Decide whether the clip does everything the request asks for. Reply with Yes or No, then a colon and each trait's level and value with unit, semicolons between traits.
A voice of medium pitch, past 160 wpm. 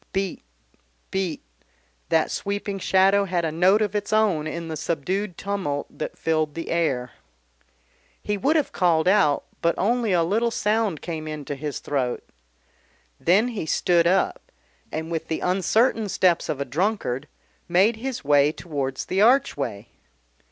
No: medium, 180 Hz; average, 150 wpm